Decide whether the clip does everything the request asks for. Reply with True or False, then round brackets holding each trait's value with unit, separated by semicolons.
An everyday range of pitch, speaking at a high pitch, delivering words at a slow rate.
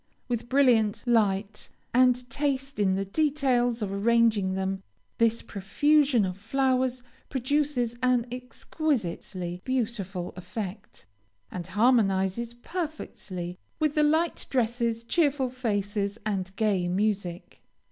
True (4.7 semitones; 230 Hz; 105 wpm)